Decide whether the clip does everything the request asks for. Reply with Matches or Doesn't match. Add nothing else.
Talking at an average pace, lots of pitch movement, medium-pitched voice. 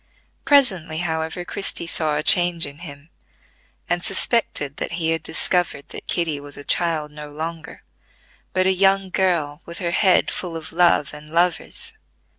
Doesn't match